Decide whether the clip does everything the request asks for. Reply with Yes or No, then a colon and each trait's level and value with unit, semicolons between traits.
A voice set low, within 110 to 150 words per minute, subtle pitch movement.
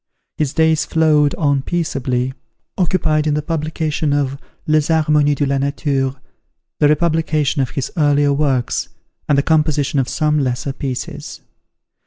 No: medium, 145 Hz; average, 140 wpm; narrow, 2.0 semitones